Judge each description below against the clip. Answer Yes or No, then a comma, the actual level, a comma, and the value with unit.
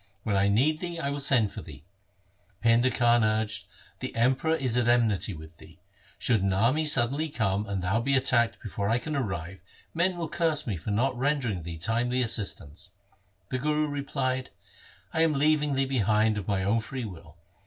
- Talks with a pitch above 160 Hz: No, low, 120 Hz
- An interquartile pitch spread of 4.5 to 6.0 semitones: Yes, wide, 5.5 semitones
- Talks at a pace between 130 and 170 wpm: No, average, 195 wpm